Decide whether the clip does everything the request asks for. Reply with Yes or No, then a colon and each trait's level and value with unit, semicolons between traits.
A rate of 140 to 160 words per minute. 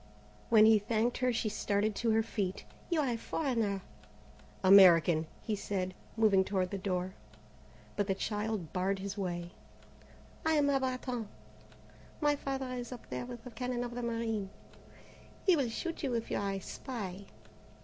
No: average, 170 wpm